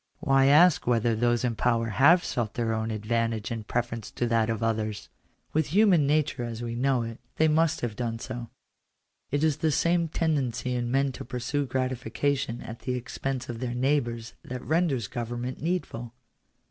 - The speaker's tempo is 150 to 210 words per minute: Yes, average, 175 wpm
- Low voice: Yes, low, 125 Hz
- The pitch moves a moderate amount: Yes, average, 3.5 semitones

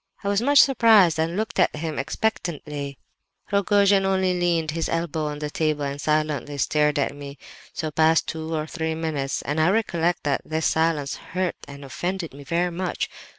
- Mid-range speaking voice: Yes, medium, 160 Hz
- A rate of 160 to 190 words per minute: Yes, average, 180 wpm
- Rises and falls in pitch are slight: No, average, 3.4 semitones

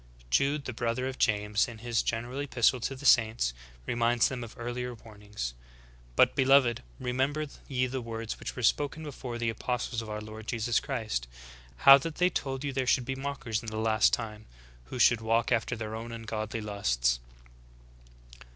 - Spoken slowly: No, average, 190 wpm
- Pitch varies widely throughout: No, average, 3.0 semitones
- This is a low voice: Yes, low, 120 Hz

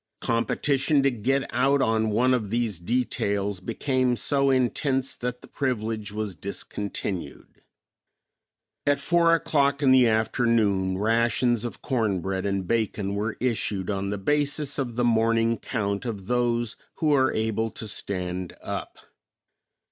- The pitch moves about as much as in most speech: Yes, average, 4.2 semitones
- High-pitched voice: No, low, 115 Hz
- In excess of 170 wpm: No, average, 140 wpm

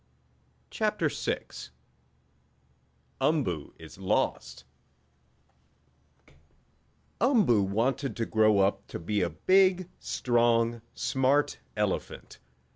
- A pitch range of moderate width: No, wide, 6.1 semitones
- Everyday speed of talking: No, slow, 80 wpm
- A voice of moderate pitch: No, low, 115 Hz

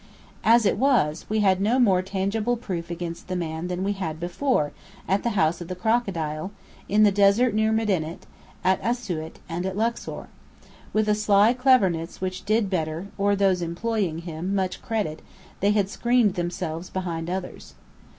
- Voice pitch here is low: No, high, 190 Hz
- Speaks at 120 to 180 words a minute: Yes, average, 170 wpm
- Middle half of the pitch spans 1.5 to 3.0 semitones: No, average, 3.8 semitones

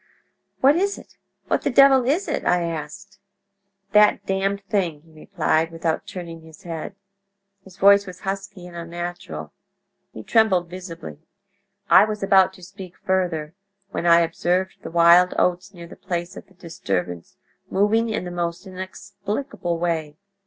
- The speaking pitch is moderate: Yes, medium, 180 Hz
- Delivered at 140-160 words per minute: Yes, average, 150 wpm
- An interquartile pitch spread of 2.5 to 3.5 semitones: Yes, average, 2.9 semitones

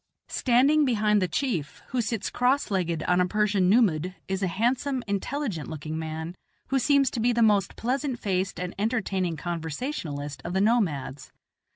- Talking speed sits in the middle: Yes, average, 165 wpm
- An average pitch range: No, wide, 6.2 semitones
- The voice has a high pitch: Yes, high, 200 Hz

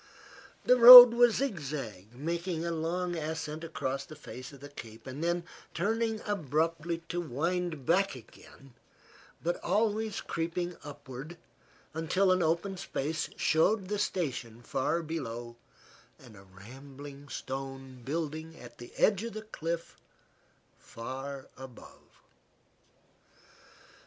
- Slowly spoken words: Yes, slow, 115 wpm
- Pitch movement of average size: Yes, average, 5.0 semitones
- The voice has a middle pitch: Yes, medium, 160 Hz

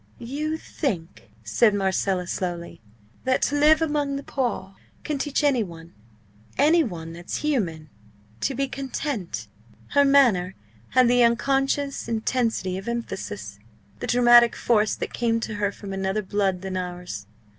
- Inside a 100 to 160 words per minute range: Yes, average, 145 wpm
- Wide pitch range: Yes, wide, 6.8 semitones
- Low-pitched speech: No, high, 230 Hz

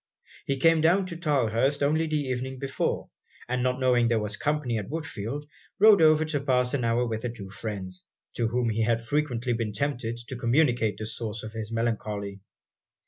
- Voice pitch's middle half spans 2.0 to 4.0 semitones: No, average, 4.5 semitones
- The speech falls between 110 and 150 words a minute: No, average, 190 wpm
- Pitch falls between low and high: No, low, 125 Hz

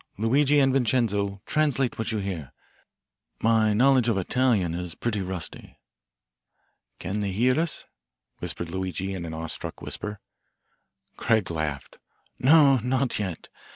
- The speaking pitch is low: Yes, low, 105 Hz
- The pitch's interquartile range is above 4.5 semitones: Yes, wide, 5.6 semitones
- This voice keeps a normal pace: No, slow, 130 wpm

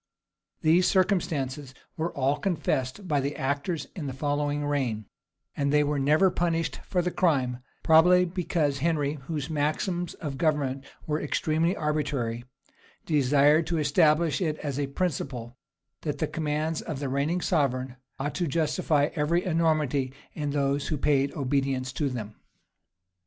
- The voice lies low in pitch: No, medium, 150 Hz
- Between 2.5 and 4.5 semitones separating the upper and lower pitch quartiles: Yes, average, 2.9 semitones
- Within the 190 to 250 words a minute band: No, average, 145 wpm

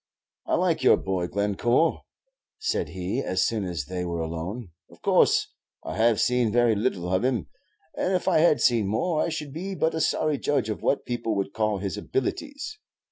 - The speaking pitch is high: No, low, 110 Hz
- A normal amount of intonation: No, wide, 7.6 semitones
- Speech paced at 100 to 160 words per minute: No, average, 190 wpm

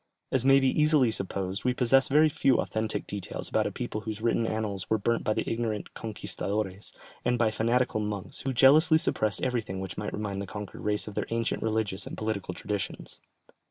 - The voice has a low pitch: Yes, low, 110 Hz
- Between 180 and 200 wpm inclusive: Yes, average, 195 wpm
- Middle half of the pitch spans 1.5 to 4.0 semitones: Yes, average, 3.1 semitones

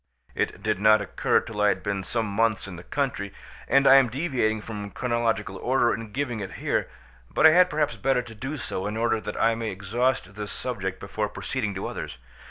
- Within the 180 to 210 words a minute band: Yes, fast, 205 wpm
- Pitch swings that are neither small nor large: Yes, average, 3.9 semitones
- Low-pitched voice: Yes, low, 110 Hz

